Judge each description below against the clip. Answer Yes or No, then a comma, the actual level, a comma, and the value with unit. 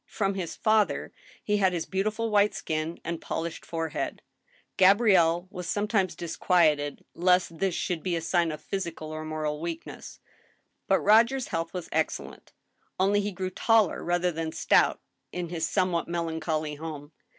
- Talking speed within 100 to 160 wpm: Yes, average, 150 wpm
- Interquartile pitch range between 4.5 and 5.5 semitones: No, average, 3.2 semitones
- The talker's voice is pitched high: No, medium, 175 Hz